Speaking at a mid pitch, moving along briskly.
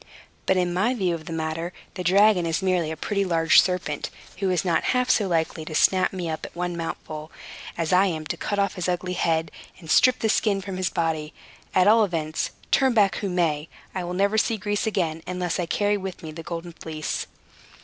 Yes: medium, 180 Hz; fast, 220 wpm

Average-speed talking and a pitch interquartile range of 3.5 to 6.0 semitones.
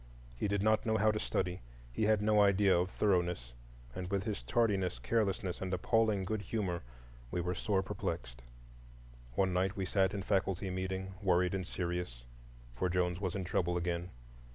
No: average, 175 wpm; narrow, 2.4 semitones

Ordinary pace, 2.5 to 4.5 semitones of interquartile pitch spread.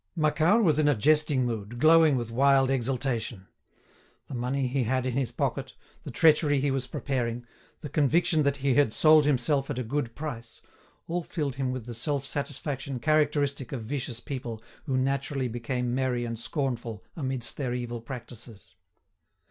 Yes: average, 165 wpm; average, 3.2 semitones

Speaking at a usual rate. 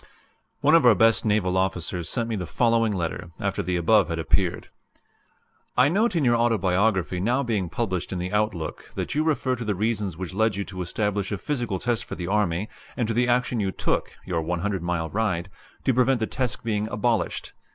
No: fast, 210 wpm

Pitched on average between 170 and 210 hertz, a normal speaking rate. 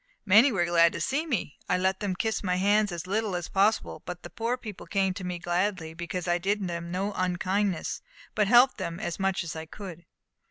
No: medium, 185 Hz; fast, 215 wpm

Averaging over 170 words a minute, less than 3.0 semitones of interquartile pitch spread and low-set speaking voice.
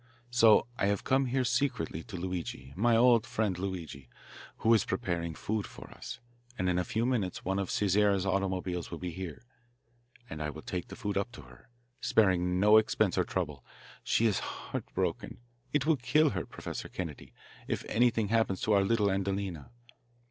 No: average, 180 wpm; average, 3.8 semitones; very low, 95 Hz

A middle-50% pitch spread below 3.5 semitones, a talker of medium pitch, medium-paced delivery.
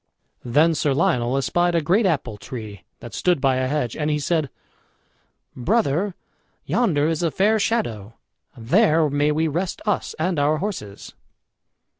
No: average, 5.2 semitones; medium, 150 Hz; average, 150 wpm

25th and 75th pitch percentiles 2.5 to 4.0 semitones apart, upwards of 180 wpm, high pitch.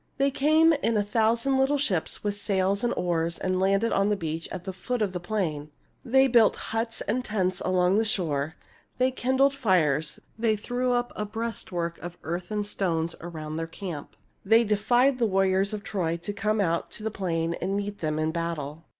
No: average, 5.1 semitones; average, 195 wpm; high, 200 Hz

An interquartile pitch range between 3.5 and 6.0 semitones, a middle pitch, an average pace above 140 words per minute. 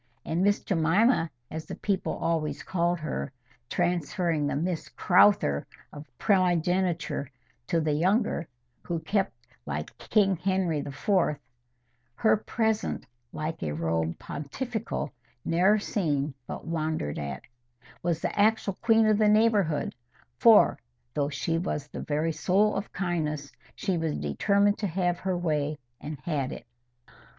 No: average, 4.7 semitones; medium, 170 Hz; slow, 135 wpm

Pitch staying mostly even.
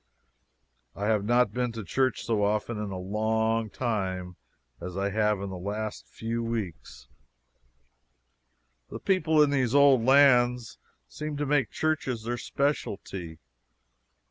No: average, 4.3 semitones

